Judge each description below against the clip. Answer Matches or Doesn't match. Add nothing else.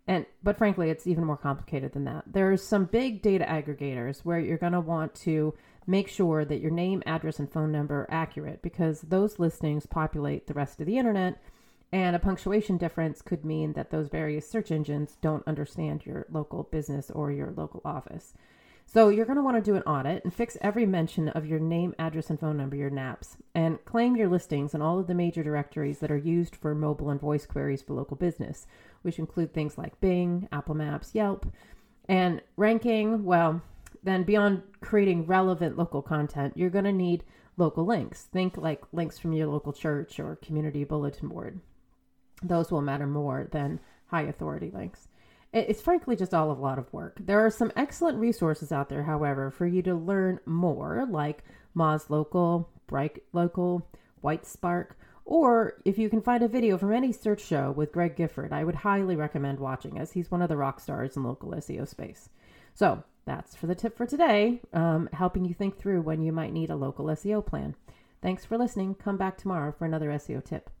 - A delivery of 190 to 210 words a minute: Matches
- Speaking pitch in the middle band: Matches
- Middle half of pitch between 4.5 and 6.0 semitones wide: Doesn't match